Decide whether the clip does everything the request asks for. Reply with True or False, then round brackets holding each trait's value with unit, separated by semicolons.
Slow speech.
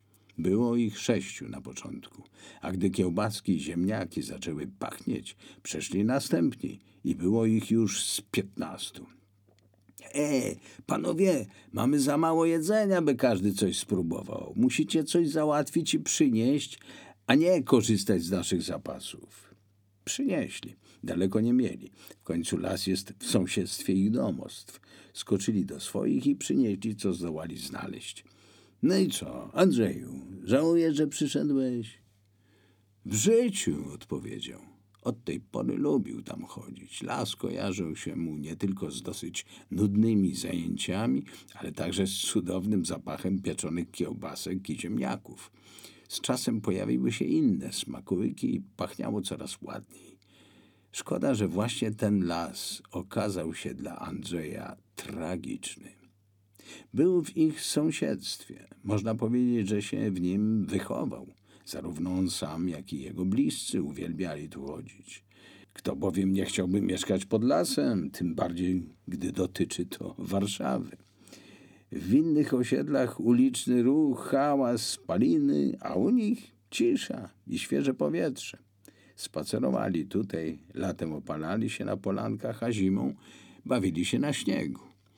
False (125 wpm)